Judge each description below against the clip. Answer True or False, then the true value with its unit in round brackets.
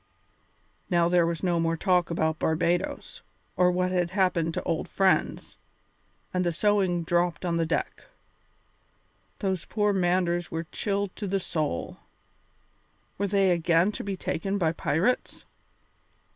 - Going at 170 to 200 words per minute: False (140 wpm)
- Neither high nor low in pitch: True (175 Hz)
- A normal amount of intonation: False (2.3 semitones)